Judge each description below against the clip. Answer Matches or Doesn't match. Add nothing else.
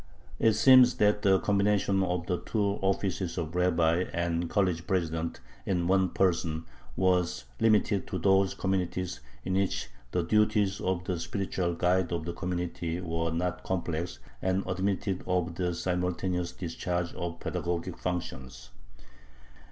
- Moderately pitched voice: Doesn't match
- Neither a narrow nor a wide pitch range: Doesn't match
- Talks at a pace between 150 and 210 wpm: Doesn't match